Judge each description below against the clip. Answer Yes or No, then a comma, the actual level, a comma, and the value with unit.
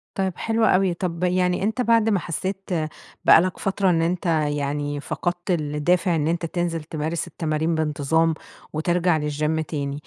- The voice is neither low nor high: Yes, medium, 170 Hz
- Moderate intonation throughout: Yes, average, 3.1 semitones